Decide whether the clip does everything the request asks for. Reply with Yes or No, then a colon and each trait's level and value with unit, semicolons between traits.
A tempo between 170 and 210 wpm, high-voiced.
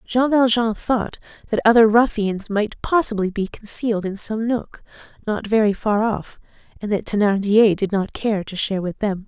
Yes: average, 175 wpm; high, 215 Hz